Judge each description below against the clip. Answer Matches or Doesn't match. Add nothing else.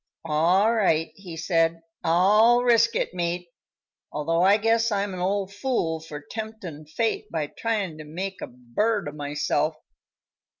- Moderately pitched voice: Matches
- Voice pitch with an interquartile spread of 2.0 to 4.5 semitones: Doesn't match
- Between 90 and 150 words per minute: Matches